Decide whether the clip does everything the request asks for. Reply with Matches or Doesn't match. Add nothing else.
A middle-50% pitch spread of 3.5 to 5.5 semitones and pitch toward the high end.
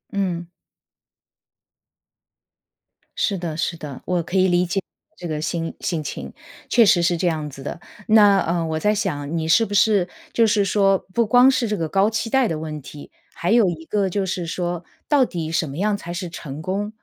Doesn't match